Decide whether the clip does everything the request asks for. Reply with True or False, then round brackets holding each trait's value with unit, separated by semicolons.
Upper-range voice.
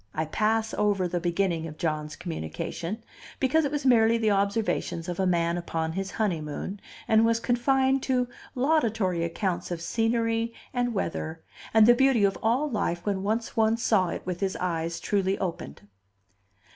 True (200 Hz)